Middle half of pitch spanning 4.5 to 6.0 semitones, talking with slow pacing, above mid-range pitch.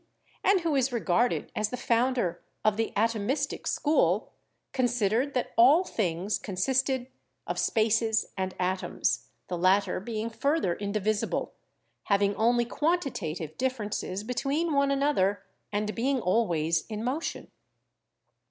Yes: average, 4.8 semitones; slow, 125 wpm; high, 225 Hz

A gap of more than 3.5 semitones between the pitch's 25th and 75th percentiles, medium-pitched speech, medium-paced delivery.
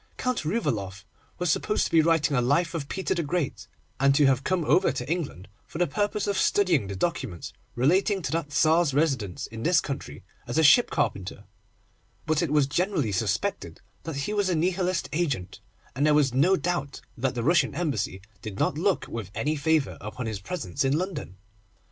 Yes: average, 5.2 semitones; medium, 150 Hz; average, 190 wpm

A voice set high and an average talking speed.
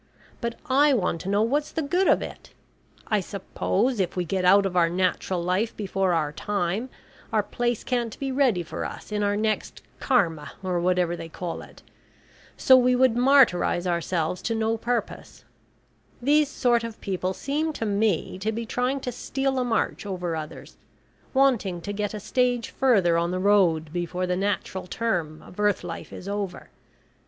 Yes: high, 205 Hz; average, 180 wpm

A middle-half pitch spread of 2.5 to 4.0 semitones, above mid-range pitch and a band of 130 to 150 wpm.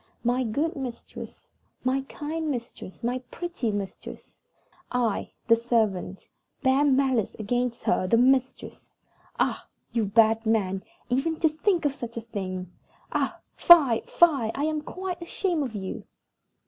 No: average, 4.8 semitones; high, 245 Hz; slow, 135 wpm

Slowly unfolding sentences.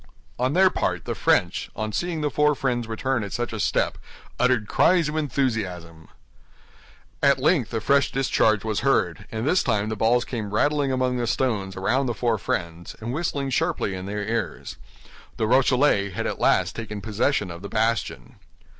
No: average, 180 wpm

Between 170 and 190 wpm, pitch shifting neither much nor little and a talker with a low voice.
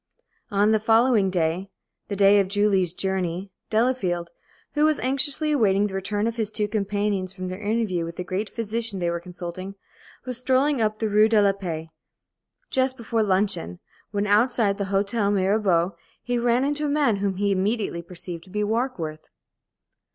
No: average, 175 wpm; average, 3.4 semitones; high, 205 Hz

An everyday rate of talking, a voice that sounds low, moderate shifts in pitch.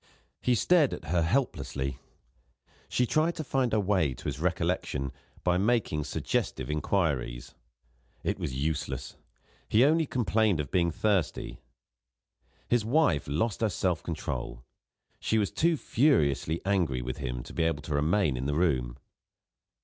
No: average, 145 wpm; very low, 90 Hz; wide, 8.0 semitones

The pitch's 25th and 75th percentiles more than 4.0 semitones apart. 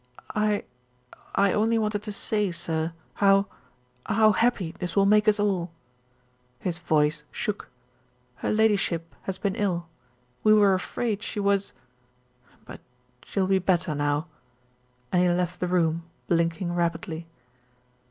No: average, 3.5 semitones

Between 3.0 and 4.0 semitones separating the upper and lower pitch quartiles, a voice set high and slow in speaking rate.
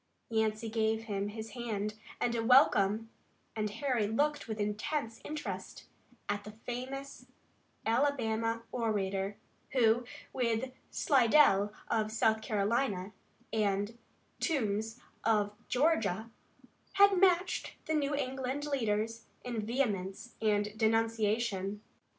Yes: average, 3.3 semitones; high, 225 Hz; slow, 105 wpm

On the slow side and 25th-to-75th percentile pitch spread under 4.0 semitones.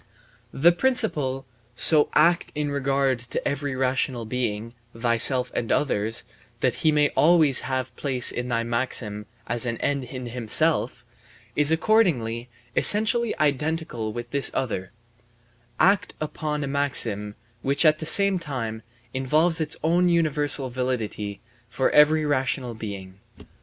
No: slow, 130 wpm; average, 4.4 semitones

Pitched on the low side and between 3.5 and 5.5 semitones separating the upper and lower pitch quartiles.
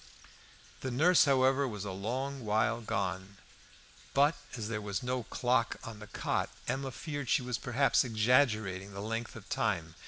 Yes: low, 115 Hz; average, 3.9 semitones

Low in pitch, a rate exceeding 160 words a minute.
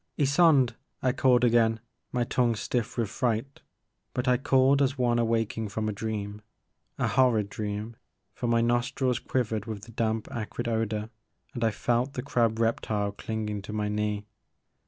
Yes: low, 115 Hz; average, 175 wpm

